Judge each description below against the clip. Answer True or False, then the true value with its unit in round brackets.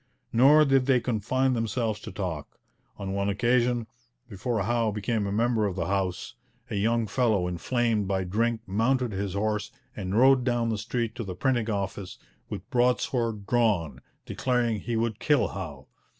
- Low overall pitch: True (110 Hz)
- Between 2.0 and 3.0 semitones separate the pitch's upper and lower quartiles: False (3.4 semitones)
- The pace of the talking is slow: False (165 wpm)